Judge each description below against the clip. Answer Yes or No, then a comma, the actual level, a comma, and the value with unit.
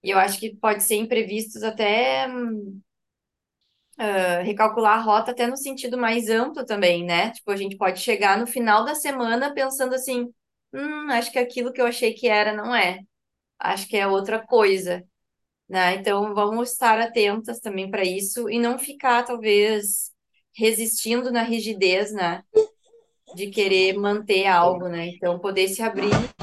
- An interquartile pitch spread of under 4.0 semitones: Yes, average, 3.5 semitones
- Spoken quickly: No, average, 160 wpm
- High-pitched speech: Yes, high, 220 Hz